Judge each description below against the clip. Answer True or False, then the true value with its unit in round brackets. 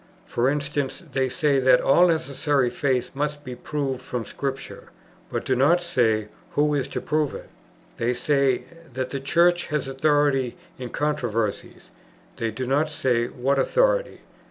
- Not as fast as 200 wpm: True (155 wpm)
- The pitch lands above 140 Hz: False (135 Hz)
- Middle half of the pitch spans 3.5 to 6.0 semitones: False (2.8 semitones)